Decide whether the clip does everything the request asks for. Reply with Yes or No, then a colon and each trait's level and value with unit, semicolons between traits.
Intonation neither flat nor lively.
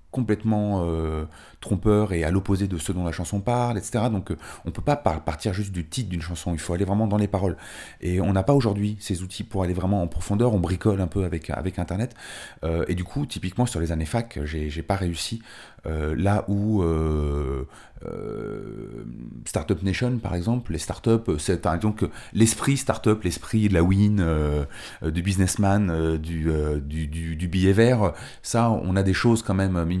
Yes: average, 4.2 semitones